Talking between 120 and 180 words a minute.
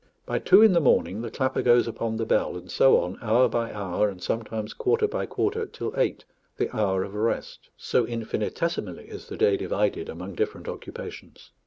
No: average, 190 wpm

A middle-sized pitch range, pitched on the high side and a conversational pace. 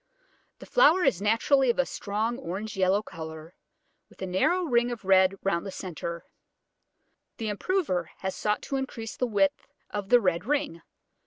Yes: average, 4.7 semitones; high, 205 Hz; average, 165 wpm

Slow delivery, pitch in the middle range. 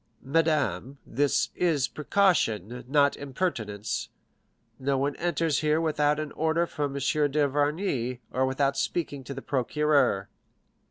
Yes: slow, 120 wpm; medium, 145 Hz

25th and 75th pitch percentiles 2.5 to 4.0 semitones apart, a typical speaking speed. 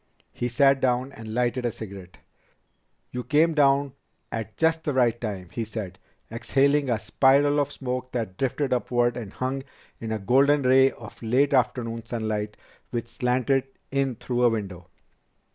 Yes: average, 3.3 semitones; average, 160 wpm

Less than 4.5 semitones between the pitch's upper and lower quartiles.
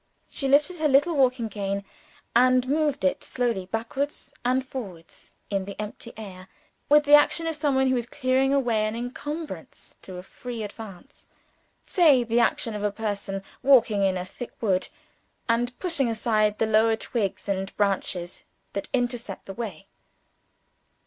No: average, 4.9 semitones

